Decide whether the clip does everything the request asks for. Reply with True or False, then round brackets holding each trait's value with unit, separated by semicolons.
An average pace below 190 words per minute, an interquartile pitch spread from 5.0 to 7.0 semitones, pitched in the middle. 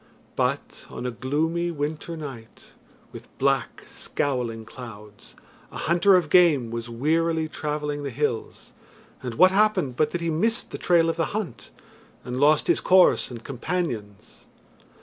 True (150 wpm; 5.4 semitones; 150 Hz)